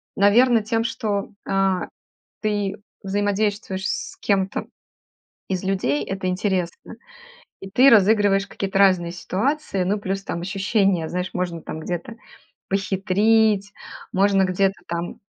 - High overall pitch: Yes, high, 195 Hz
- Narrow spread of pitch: Yes, narrow, 1.8 semitones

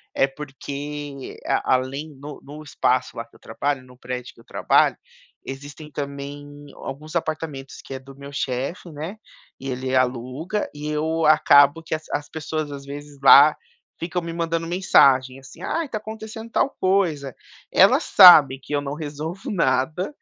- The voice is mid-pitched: Yes, medium, 145 Hz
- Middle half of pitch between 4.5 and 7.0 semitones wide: No, average, 3.1 semitones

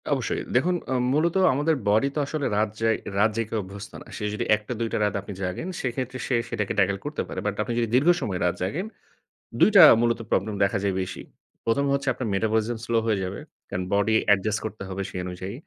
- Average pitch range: Yes, average, 4.5 semitones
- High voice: No, low, 110 Hz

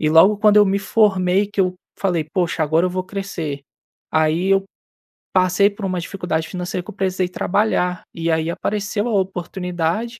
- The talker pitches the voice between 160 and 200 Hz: Yes, medium, 185 Hz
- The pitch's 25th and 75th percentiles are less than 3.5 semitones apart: Yes, average, 2.8 semitones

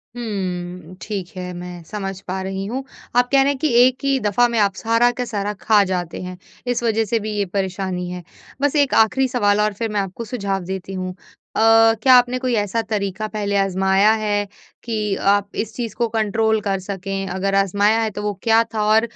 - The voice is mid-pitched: No, high, 205 Hz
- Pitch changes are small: No, average, 3.1 semitones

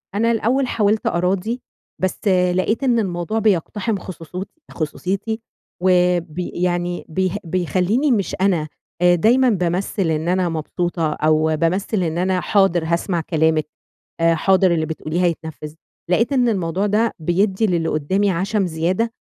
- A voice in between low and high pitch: Yes, medium, 180 Hz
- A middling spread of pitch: Yes, average, 3.5 semitones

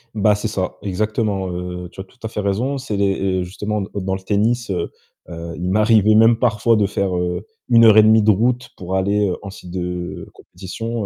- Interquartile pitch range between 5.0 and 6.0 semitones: No, average, 2.8 semitones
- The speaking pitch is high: No, low, 100 Hz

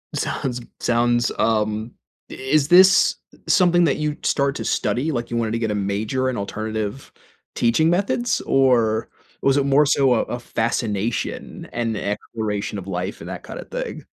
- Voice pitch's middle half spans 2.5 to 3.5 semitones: No, average, 4.1 semitones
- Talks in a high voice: No, low, 120 Hz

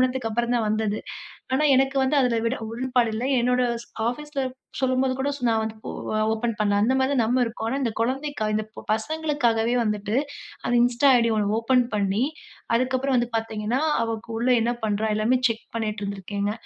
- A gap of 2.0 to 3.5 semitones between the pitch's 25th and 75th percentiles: Yes, average, 2.9 semitones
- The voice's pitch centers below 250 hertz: Yes, high, 230 Hz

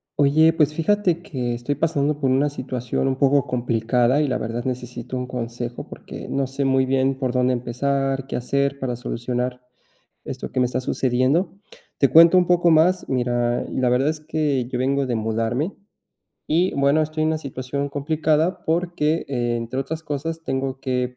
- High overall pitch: No, low, 135 Hz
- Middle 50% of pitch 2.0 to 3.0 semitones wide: No, average, 3.4 semitones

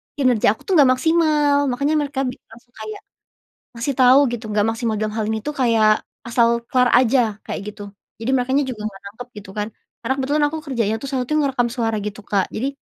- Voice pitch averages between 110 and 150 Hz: No, high, 245 Hz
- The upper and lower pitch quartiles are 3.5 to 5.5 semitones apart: Yes, average, 3.9 semitones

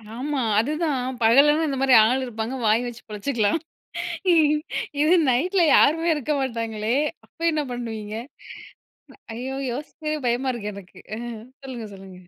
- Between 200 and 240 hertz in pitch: No, very high, 250 Hz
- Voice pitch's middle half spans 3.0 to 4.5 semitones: No, average, 4.9 semitones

